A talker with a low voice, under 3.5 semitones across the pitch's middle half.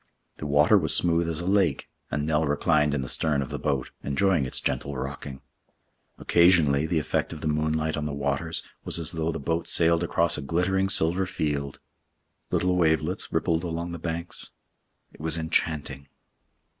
Yes: very low, 80 Hz; narrow, 2.6 semitones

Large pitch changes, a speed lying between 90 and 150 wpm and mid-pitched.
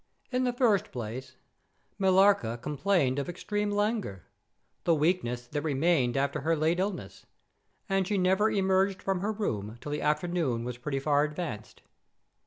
Yes: wide, 6.3 semitones; average, 140 wpm; medium, 165 Hz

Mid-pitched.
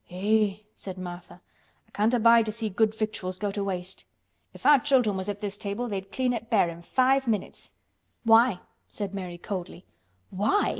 No: high, 205 Hz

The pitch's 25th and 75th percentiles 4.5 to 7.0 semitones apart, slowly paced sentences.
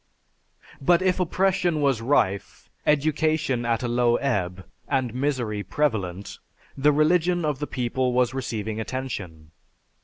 Yes: average, 5.2 semitones; slow, 125 wpm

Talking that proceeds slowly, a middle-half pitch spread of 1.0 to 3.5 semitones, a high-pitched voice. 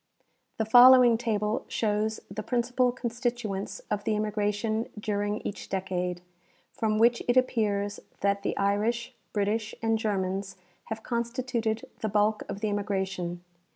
Yes: slow, 130 wpm; narrow, 2.5 semitones; high, 215 Hz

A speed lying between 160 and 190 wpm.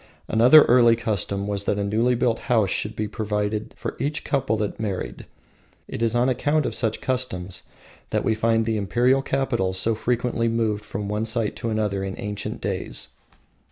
Yes: average, 180 wpm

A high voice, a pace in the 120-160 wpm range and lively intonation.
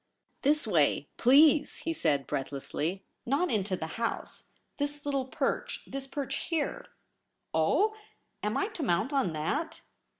Yes: very high, 270 Hz; average, 155 wpm; wide, 8.6 semitones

